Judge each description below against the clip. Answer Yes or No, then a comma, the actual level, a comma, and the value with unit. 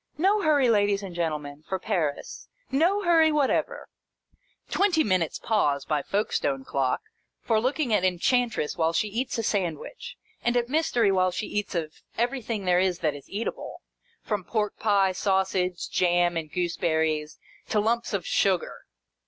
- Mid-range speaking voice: No, high, 195 Hz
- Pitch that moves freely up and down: Yes, wide, 5.7 semitones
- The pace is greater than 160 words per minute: No, average, 155 wpm